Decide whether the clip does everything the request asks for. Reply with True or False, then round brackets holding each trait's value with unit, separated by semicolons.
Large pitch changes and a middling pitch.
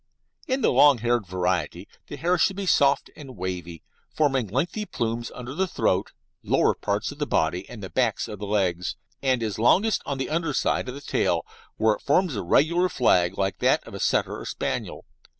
False (7.2 semitones; 120 Hz)